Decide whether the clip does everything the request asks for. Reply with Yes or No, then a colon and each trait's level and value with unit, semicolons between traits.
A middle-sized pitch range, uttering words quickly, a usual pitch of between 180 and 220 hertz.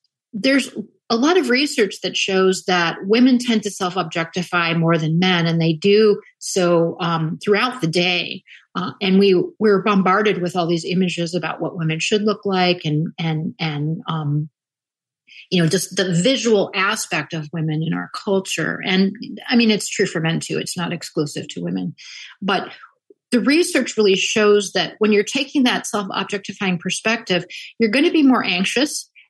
No: average, 4.2 semitones; average, 170 wpm; medium, 185 Hz